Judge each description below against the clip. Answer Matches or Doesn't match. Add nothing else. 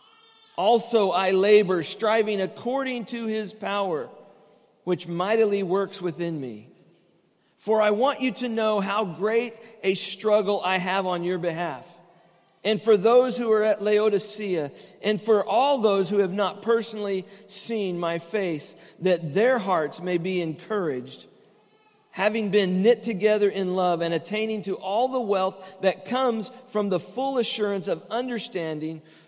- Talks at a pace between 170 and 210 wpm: Doesn't match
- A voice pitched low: Doesn't match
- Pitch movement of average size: Matches